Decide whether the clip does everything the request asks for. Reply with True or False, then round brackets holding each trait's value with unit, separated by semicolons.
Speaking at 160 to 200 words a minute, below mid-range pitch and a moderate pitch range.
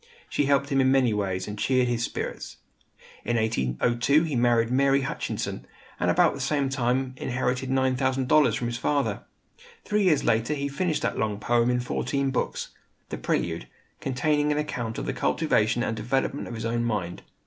True (175 wpm; 130 Hz; 3.0 semitones)